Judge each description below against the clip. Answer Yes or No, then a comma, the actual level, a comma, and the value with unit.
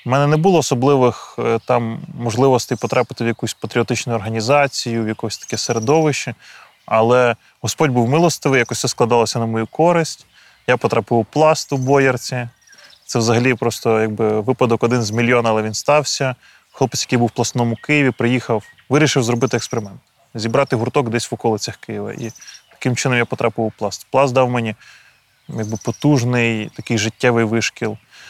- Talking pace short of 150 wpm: No, fast, 155 wpm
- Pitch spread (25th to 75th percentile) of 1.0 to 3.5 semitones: Yes, narrow, 2.5 semitones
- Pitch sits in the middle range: No, low, 120 Hz